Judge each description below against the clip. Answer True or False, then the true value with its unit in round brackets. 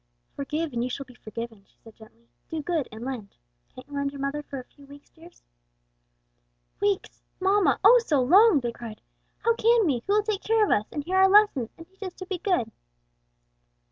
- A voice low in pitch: False (295 Hz)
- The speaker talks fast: True (210 wpm)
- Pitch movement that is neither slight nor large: False (7.6 semitones)